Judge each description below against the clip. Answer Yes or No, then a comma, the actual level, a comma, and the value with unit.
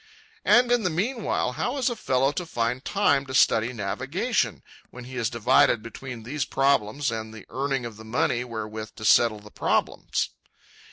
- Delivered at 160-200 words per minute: Yes, average, 170 wpm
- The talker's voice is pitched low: Yes, low, 125 Hz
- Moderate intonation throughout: Yes, average, 4.3 semitones